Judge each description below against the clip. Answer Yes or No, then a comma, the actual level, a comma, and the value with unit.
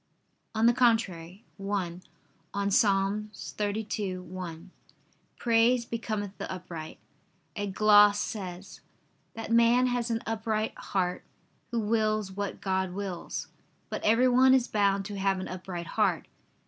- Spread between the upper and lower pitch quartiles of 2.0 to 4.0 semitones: Yes, average, 3.0 semitones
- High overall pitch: Yes, high, 205 Hz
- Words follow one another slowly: Yes, slow, 120 wpm